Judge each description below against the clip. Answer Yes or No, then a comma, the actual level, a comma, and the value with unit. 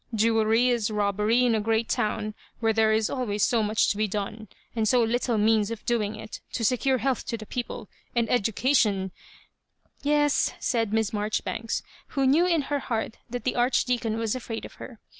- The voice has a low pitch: No, high, 225 Hz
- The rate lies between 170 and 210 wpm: Yes, average, 195 wpm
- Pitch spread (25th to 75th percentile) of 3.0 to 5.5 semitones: No, narrow, 2.5 semitones